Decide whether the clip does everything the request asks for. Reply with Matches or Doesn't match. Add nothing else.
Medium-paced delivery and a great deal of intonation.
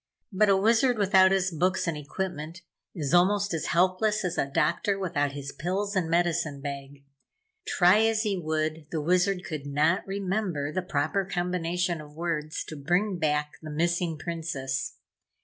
Doesn't match